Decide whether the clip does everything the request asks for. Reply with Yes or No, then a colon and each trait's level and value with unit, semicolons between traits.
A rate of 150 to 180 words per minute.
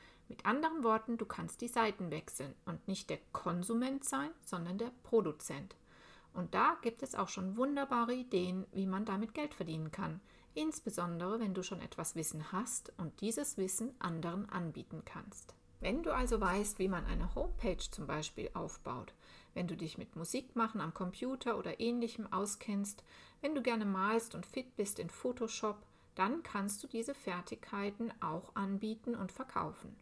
Yes: average, 165 wpm